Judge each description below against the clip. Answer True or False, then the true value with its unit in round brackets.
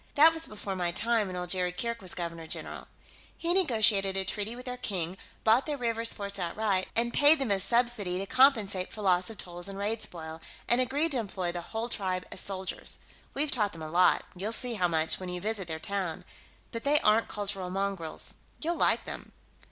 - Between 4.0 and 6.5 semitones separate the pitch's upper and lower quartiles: True (4.6 semitones)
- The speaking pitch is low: False (200 Hz)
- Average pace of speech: False (210 wpm)